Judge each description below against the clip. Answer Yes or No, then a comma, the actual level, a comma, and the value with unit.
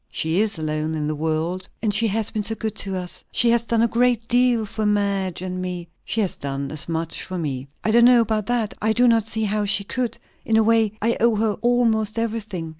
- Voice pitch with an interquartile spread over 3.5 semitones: Yes, average, 4.1 semitones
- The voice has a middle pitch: No, high, 215 Hz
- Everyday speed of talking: No, fast, 240 wpm